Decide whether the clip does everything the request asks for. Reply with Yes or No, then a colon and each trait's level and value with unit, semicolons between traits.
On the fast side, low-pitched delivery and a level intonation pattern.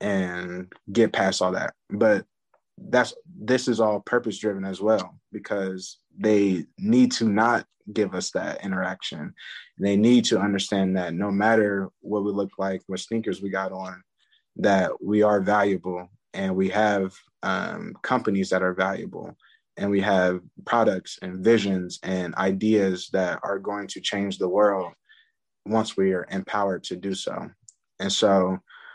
No: average, 155 wpm; low, 100 Hz; narrow, 2.0 semitones